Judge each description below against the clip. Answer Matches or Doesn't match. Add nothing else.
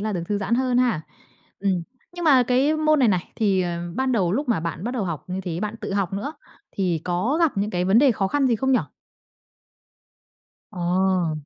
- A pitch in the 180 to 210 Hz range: Matches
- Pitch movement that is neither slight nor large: Doesn't match